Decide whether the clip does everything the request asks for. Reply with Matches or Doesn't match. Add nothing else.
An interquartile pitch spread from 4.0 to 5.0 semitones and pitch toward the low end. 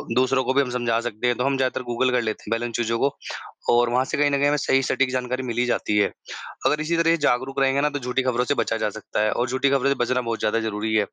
Doesn't match